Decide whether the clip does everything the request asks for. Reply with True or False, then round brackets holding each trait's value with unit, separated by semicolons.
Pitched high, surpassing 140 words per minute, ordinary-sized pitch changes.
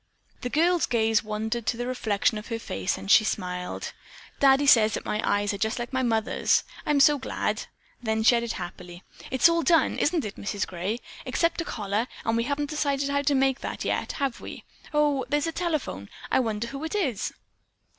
True (240 Hz; 195 wpm; 5.0 semitones)